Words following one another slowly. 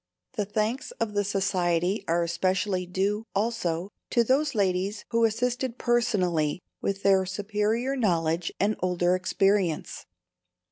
Yes: slow, 125 wpm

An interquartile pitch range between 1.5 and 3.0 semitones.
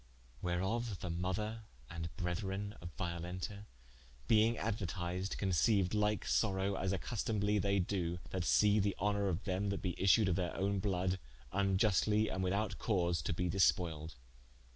Yes: average, 2.7 semitones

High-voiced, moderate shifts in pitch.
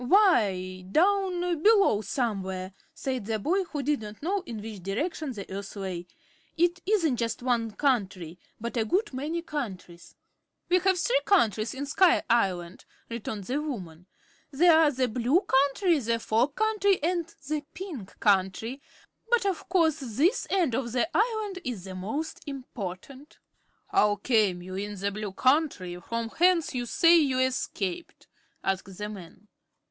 No: very high, 255 Hz; wide, 8.5 semitones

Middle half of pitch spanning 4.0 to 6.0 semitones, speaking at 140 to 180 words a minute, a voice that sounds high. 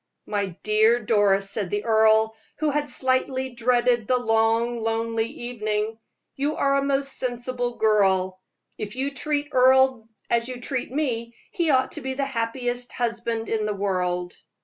No: average, 3.0 semitones; average, 155 wpm; high, 235 Hz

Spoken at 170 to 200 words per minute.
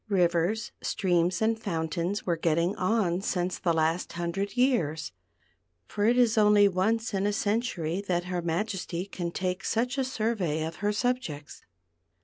No: average, 150 wpm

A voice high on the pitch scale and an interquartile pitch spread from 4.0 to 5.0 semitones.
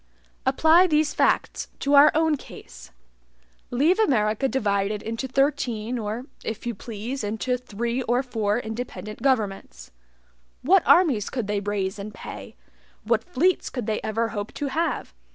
Yes: high, 235 Hz; average, 4.5 semitones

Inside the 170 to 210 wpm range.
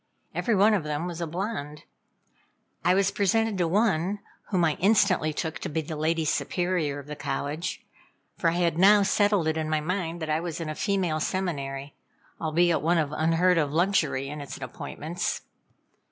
Yes: average, 180 wpm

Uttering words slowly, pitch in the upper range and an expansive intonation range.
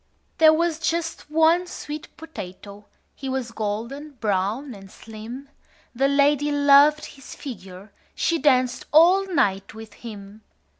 Yes: slow, 130 wpm; very high, 270 Hz; wide, 6.2 semitones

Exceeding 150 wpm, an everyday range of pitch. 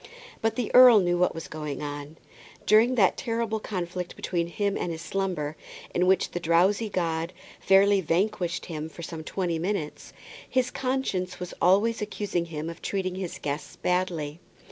Yes: average, 165 wpm; average, 3.7 semitones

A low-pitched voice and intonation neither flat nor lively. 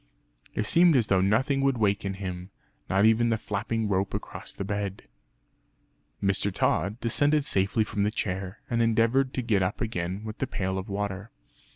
Yes: low, 105 Hz; average, 3.2 semitones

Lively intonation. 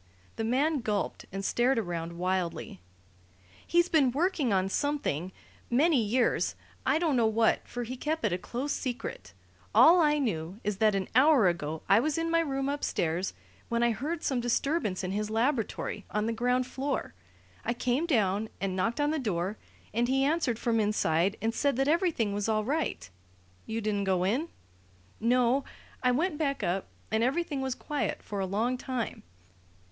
Yes: wide, 5.8 semitones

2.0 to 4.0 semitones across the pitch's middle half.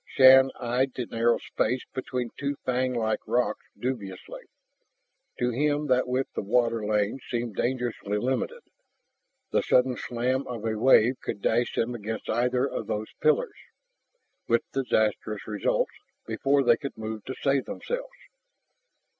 Yes: average, 2.9 semitones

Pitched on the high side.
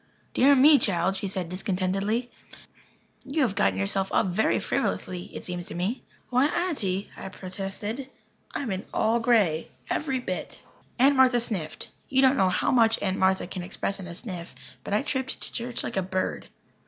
Yes: high, 200 Hz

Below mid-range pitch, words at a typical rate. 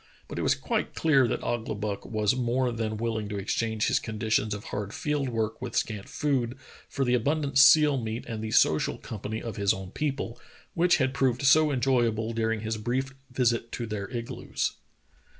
Yes: low, 115 Hz; average, 185 wpm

